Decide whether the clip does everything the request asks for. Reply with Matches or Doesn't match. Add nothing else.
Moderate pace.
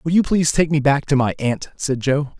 Doesn't match